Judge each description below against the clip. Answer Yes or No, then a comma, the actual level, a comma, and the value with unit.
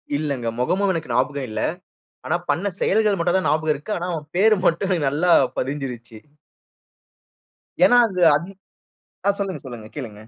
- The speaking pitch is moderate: Yes, medium, 155 Hz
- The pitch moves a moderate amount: No, wide, 6.0 semitones